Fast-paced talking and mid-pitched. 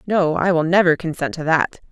Yes: fast, 220 wpm; medium, 170 Hz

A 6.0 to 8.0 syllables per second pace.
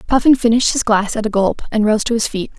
Yes: 6.5 syllables/s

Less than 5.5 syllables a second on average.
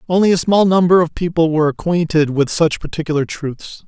No: 5.7 syllables/s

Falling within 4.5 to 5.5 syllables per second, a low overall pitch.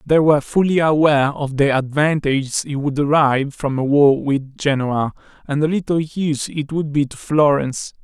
No: 5.1 syllables/s; medium, 145 Hz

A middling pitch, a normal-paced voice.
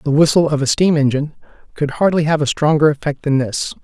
No: medium, 150 Hz; fast, 220 wpm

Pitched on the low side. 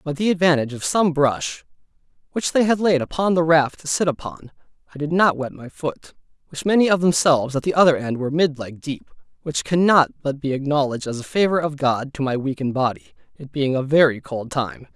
No: medium, 150 Hz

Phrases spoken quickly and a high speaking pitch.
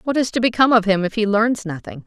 Yes: fast, 290 wpm; high, 220 Hz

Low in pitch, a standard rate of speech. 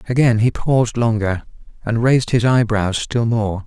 Yes: low, 115 Hz; average, 165 wpm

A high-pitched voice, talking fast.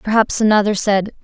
No: high, 210 Hz; average, 145 wpm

